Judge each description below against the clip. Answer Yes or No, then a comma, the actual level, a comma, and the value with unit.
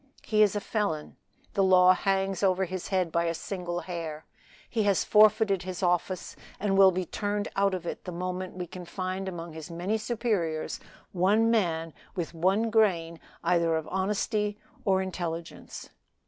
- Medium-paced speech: Yes, average, 165 wpm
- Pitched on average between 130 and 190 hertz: Yes, medium, 185 Hz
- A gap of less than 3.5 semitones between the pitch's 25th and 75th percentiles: Yes, average, 2.8 semitones